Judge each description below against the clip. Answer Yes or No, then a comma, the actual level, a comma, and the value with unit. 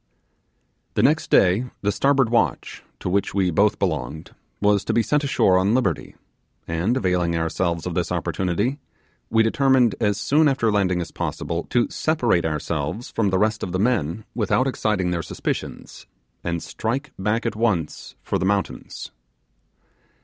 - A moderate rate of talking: Yes, average, 155 wpm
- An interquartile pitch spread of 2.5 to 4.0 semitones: No, average, 5.0 semitones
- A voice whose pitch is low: Yes, low, 100 Hz